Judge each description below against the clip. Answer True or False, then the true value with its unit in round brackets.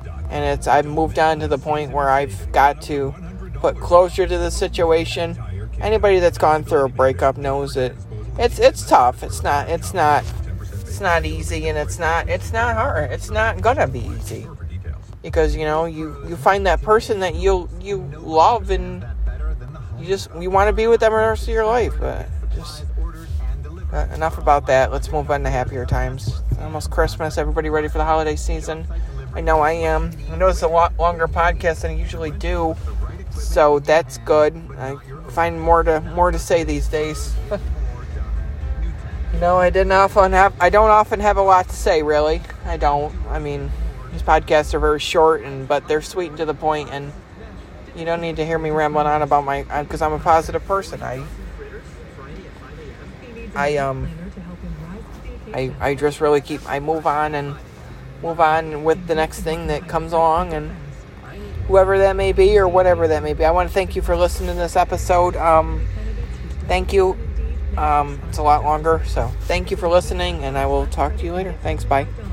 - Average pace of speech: True (190 wpm)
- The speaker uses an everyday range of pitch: False (9.0 semitones)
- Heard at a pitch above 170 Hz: False (150 Hz)